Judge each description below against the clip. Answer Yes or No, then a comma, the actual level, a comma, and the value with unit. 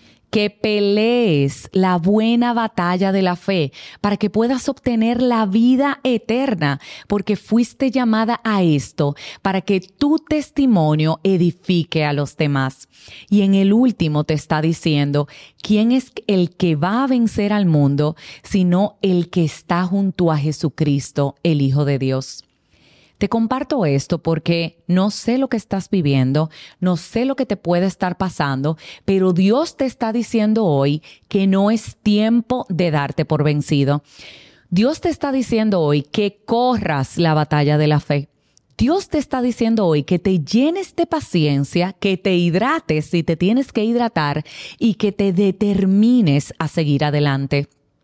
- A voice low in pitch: No, medium, 185 Hz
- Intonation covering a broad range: Yes, wide, 6.6 semitones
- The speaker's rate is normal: Yes, average, 155 wpm